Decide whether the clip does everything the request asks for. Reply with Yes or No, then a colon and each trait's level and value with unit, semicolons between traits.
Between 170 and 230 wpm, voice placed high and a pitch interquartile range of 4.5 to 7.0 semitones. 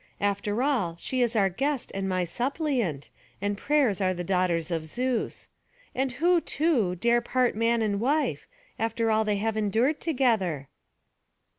No: average, 155 wpm; high, 225 Hz; average, 5.2 semitones